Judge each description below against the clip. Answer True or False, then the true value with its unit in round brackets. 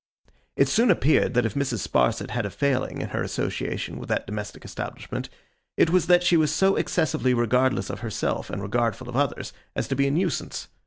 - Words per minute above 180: True (200 wpm)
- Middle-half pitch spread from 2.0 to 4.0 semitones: False (5.4 semitones)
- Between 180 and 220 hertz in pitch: False (130 Hz)